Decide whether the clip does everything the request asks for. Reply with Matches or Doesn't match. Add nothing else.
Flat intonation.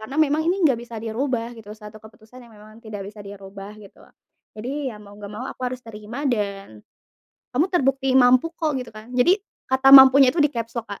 Doesn't match